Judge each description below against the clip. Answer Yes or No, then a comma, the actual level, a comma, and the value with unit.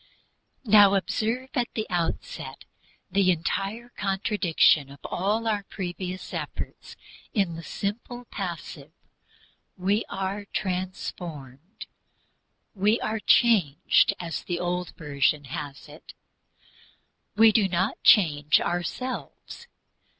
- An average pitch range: Yes, average, 4.2 semitones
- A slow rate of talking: Yes, slow, 100 wpm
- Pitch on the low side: No, high, 190 Hz